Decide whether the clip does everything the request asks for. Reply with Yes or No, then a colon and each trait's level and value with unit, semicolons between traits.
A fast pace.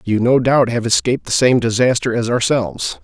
No: average, 195 wpm